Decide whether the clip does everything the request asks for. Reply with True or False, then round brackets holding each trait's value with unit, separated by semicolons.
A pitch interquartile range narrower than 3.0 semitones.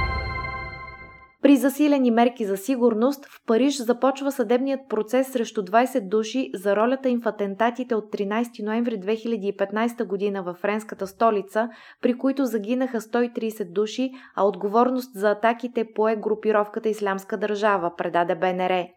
False (3.3 semitones)